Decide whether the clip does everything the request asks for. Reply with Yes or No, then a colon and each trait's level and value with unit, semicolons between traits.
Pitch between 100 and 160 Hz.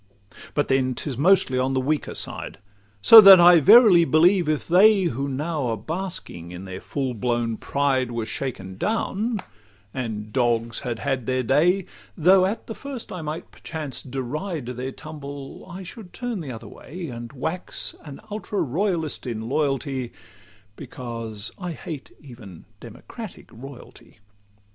Yes: medium, 140 Hz